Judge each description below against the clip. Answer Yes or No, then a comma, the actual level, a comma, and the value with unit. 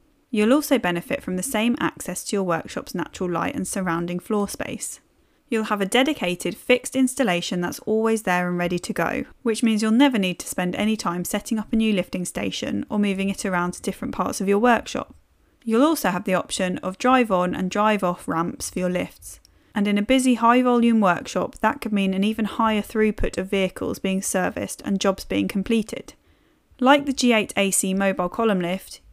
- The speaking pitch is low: No, high, 205 Hz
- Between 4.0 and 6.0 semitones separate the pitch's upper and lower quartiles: Yes, average, 4.3 semitones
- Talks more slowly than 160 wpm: No, average, 200 wpm